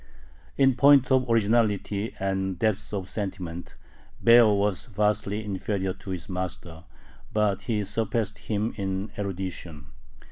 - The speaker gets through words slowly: Yes, slow, 120 wpm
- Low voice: Yes, low, 100 Hz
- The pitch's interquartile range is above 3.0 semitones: No, narrow, 2.5 semitones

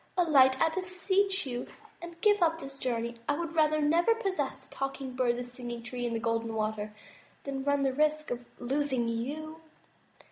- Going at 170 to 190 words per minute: Yes, average, 180 wpm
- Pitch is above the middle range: Yes, very high, 275 Hz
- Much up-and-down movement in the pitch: No, average, 4.9 semitones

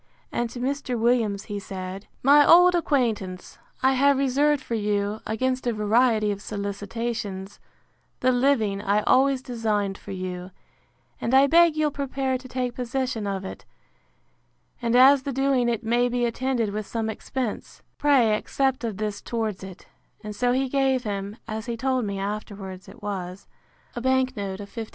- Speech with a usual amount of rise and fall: Yes, average, 4.3 semitones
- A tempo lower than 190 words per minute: Yes, average, 170 wpm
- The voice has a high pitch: Yes, high, 235 Hz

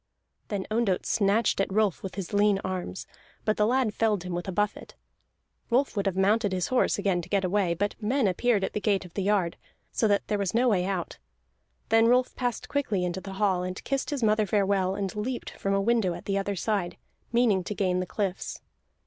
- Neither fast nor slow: No, fast, 215 wpm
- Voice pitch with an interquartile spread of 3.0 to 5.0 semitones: No, narrow, 2.6 semitones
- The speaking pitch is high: Yes, high, 200 Hz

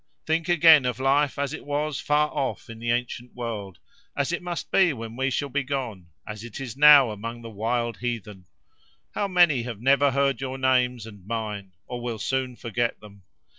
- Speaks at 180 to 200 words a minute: Yes, average, 195 wpm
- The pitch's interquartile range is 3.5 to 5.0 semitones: Yes, average, 3.8 semitones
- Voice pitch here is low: Yes, low, 125 Hz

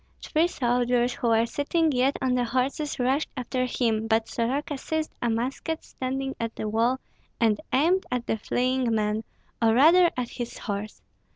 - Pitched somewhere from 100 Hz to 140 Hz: No, very high, 250 Hz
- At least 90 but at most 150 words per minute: No, average, 170 wpm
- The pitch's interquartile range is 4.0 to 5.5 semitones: No, average, 3.1 semitones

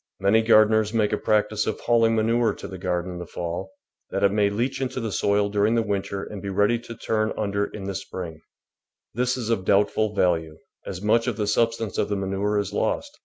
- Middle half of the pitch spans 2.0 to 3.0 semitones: Yes, narrow, 2.4 semitones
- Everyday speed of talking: No, fast, 220 wpm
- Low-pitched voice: Yes, low, 105 Hz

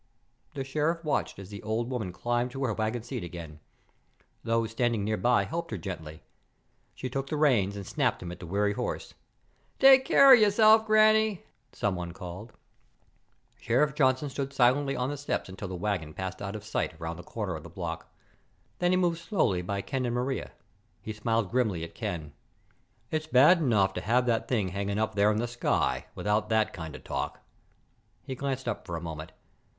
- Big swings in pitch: Yes, wide, 6.2 semitones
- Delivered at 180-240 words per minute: Yes, average, 190 wpm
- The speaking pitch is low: Yes, low, 115 Hz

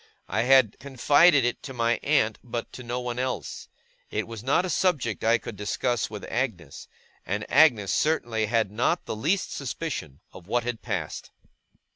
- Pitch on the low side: Yes, low, 120 Hz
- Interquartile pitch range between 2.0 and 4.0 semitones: Yes, average, 3.7 semitones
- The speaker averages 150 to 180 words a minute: Yes, average, 170 wpm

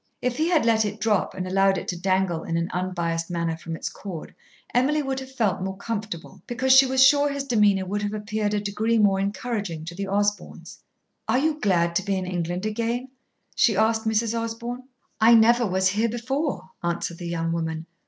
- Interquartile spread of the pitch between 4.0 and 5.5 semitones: Yes, average, 4.3 semitones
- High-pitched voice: Yes, high, 205 Hz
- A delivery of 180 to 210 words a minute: Yes, average, 200 wpm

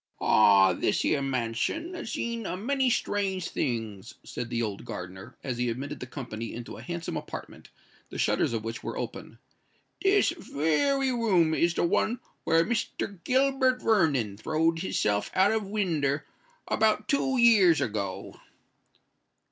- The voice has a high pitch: No, medium, 165 Hz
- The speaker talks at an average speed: Yes, average, 150 wpm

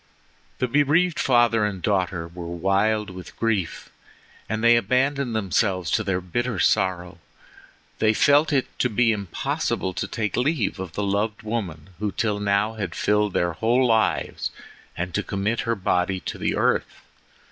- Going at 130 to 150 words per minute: No, average, 160 wpm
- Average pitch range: Yes, average, 4.0 semitones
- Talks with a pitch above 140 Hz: No, low, 105 Hz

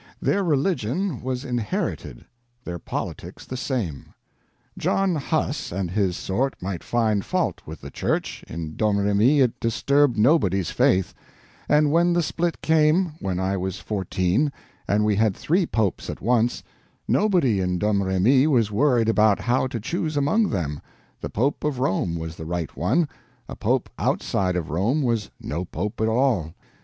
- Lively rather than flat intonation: Yes, wide, 7.2 semitones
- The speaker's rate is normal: Yes, average, 155 wpm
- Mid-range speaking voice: No, low, 110 Hz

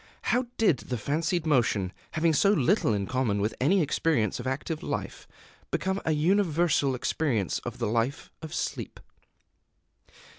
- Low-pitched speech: No, medium, 150 Hz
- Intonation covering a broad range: Yes, wide, 6.0 semitones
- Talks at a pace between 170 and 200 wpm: No, average, 145 wpm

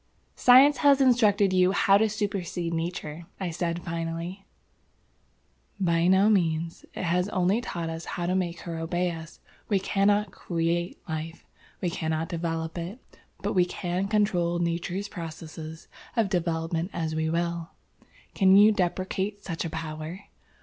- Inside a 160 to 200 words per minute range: No, average, 145 wpm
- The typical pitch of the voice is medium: Yes, medium, 175 Hz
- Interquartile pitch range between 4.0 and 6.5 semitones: No, average, 2.9 semitones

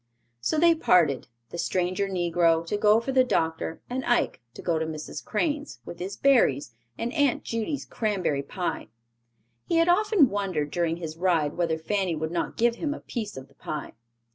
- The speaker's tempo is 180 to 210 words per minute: Yes, average, 185 wpm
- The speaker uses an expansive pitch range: Yes, wide, 7.0 semitones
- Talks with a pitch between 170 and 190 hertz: Yes, medium, 185 Hz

